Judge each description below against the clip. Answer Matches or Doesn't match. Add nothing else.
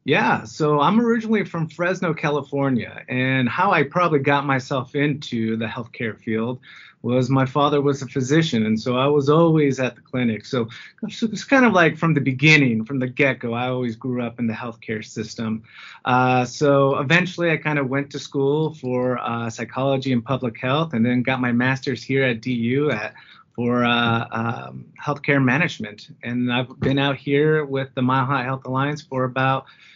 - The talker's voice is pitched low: Matches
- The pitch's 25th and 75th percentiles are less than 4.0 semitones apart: Matches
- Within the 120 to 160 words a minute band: Doesn't match